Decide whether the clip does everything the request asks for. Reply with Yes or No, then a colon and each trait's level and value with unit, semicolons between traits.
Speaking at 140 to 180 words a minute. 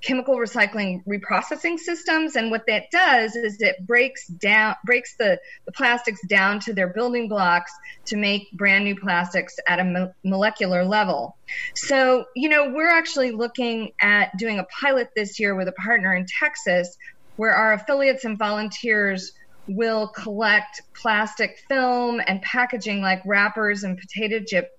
Yes: average, 155 wpm